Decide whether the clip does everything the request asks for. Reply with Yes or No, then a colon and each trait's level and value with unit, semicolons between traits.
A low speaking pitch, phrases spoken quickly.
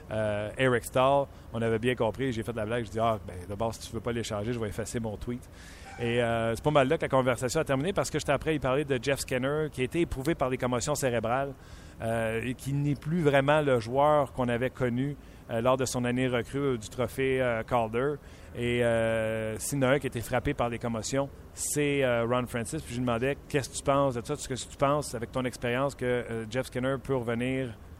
Yes: low, 125 Hz; fast, 250 wpm